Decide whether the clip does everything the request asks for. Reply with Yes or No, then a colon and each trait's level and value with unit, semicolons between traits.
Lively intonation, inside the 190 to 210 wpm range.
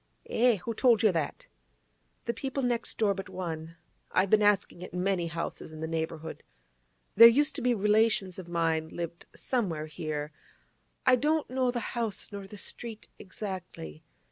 No: wide, 5.7 semitones; average, 165 wpm